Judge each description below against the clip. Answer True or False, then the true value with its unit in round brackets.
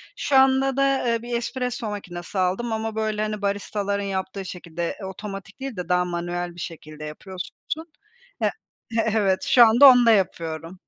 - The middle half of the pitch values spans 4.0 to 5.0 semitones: True (4.6 semitones)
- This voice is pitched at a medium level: False (200 Hz)